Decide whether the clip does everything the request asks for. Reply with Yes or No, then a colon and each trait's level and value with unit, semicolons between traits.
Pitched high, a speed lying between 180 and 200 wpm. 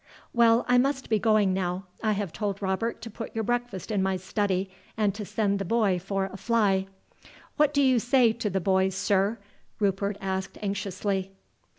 Yes: high, 200 Hz; average, 185 wpm